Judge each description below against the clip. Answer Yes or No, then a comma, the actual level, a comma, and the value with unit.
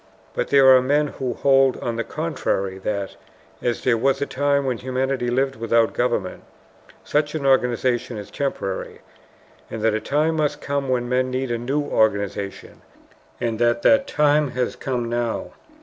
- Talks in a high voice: No, low, 130 Hz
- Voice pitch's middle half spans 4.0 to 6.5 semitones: No, average, 3.2 semitones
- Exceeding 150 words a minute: Yes, average, 165 wpm